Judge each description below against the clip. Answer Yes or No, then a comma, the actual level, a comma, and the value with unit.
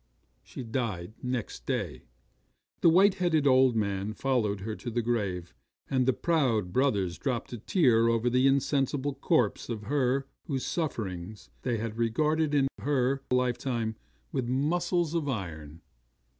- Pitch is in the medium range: No, low, 125 Hz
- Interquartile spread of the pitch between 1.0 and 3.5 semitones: No, average, 4.1 semitones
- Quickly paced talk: No, average, 145 wpm